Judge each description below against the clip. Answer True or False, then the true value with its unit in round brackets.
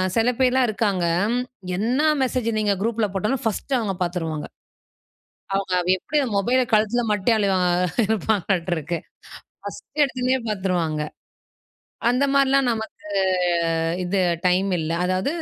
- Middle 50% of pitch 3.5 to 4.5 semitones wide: False (5.1 semitones)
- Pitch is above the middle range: True (210 Hz)